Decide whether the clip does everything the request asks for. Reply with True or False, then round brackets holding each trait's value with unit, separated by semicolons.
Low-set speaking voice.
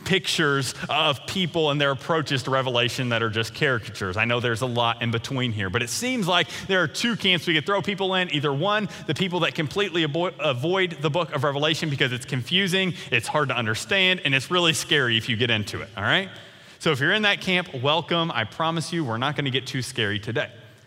False (150 Hz)